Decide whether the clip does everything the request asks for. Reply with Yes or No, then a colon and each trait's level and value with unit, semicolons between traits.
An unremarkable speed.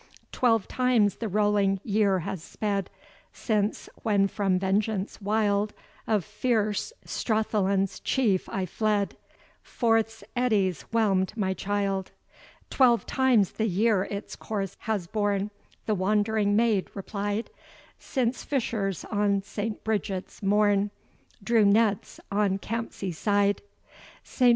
No: slow, 115 wpm